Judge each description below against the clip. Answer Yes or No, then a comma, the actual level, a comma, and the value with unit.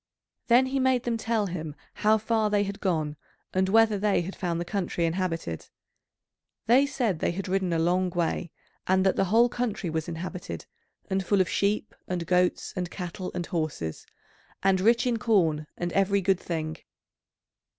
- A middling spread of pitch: Yes, average, 3.8 semitones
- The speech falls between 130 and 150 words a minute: No, average, 175 wpm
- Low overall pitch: No, high, 190 Hz